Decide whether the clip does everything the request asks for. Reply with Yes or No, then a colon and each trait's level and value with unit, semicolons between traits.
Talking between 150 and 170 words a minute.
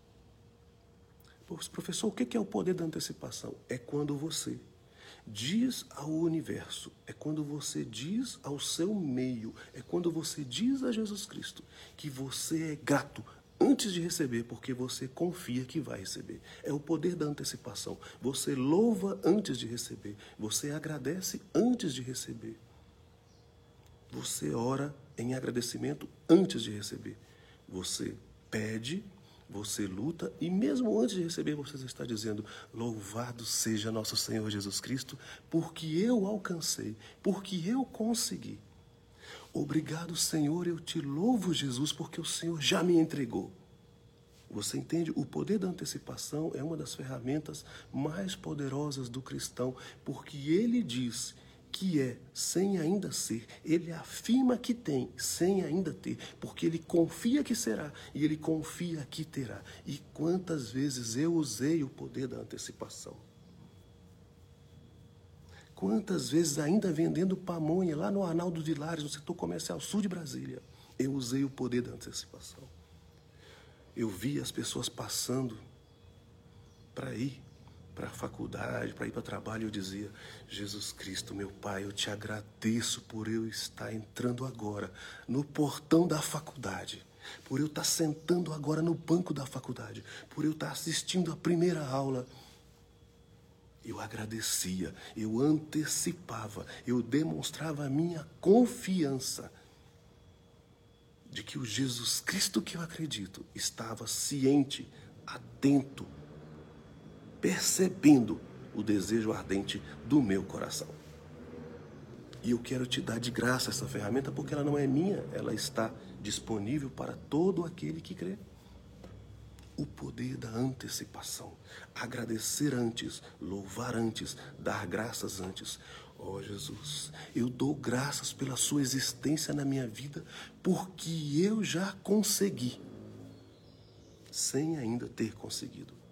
No: average, 130 wpm